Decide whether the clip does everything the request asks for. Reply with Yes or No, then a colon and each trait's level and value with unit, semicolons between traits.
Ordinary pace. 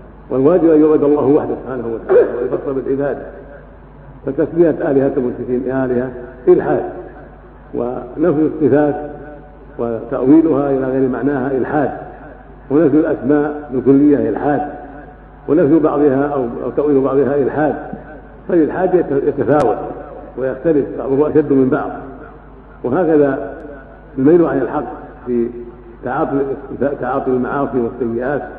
Yes: average, 95 wpm